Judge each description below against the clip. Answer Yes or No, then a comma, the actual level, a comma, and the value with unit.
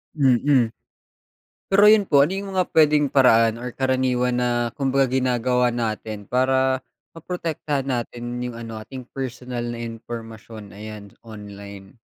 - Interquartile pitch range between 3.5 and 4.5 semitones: No, average, 3.0 semitones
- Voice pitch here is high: No, low, 125 Hz